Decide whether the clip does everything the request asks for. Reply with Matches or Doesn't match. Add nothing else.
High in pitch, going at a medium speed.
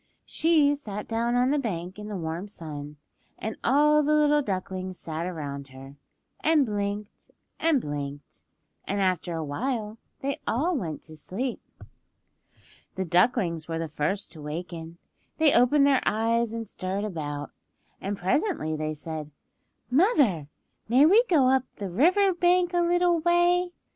Matches